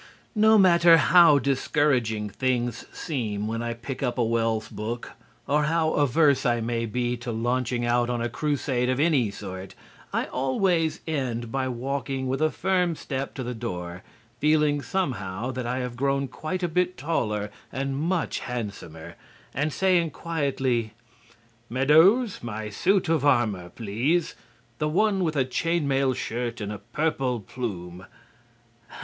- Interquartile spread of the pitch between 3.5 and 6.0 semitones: Yes, average, 4.7 semitones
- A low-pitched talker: Yes, low, 130 Hz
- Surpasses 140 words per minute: Yes, average, 150 wpm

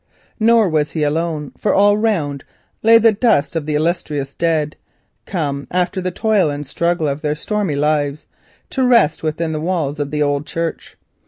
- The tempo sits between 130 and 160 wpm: No, average, 170 wpm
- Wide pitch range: No, average, 4.4 semitones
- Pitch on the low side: No, medium, 160 Hz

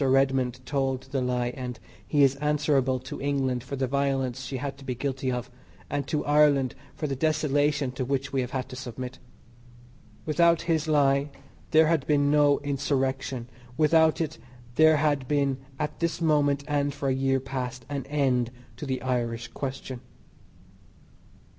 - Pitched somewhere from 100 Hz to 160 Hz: Yes, low, 135 Hz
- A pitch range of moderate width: No, narrow, 2.1 semitones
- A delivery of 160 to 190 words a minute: Yes, average, 165 wpm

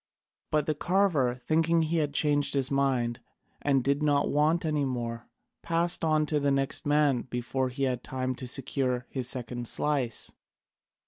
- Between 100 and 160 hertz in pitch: Yes, medium, 140 Hz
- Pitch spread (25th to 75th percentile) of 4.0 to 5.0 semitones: No, average, 3.2 semitones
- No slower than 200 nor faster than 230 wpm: No, average, 165 wpm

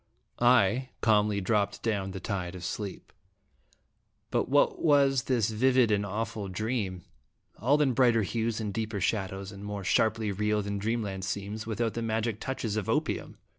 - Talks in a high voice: No, low, 110 Hz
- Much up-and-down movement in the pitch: No, narrow, 2.6 semitones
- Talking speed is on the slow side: No, average, 160 wpm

